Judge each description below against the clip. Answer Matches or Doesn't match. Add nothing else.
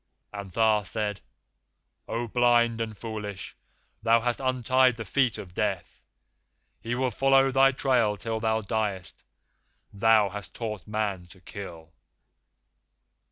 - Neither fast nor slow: Doesn't match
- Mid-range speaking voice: Doesn't match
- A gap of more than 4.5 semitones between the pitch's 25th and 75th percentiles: Doesn't match